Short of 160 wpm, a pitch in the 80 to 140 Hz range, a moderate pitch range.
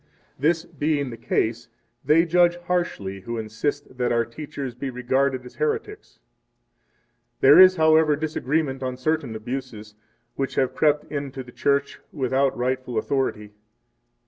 Yes: average, 140 wpm; low, 135 Hz; average, 3.9 semitones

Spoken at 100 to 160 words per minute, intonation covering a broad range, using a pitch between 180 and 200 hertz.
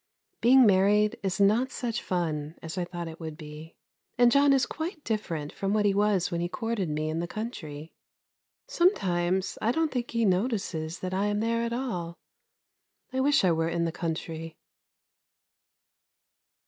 No: average, 170 wpm; wide, 5.7 semitones; high, 190 Hz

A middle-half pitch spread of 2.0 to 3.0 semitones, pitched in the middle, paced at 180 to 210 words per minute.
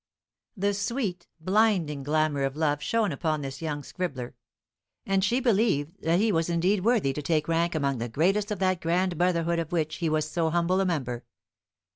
No: average, 4.2 semitones; medium, 170 Hz; average, 185 wpm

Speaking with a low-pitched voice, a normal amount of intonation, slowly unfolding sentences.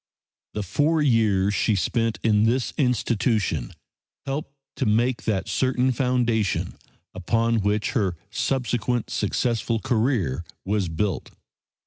Yes: low, 115 Hz; average, 3.4 semitones; slow, 110 wpm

